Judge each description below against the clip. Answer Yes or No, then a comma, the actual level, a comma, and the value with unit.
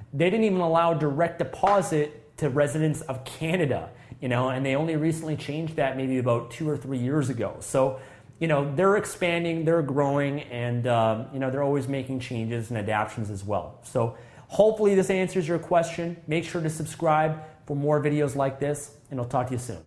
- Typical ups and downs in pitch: Yes, average, 4.1 semitones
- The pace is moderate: Yes, average, 195 wpm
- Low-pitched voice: No, medium, 145 Hz